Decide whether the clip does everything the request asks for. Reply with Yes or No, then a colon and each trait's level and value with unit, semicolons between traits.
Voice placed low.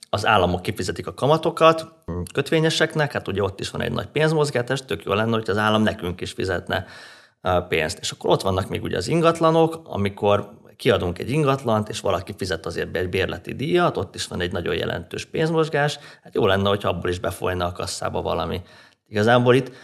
Yes: low, 110 Hz